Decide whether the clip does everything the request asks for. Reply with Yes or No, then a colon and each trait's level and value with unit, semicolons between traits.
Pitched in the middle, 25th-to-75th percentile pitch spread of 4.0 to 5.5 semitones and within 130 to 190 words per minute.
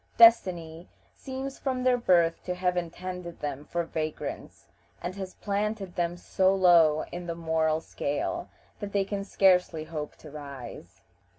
No: medium, 175 Hz; average, 3.5 semitones; average, 150 wpm